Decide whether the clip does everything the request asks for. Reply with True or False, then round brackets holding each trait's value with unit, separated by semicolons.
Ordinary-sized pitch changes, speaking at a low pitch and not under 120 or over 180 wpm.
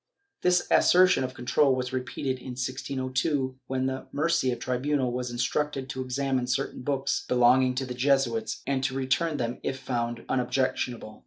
False (1.5 semitones; 130 Hz; 155 wpm)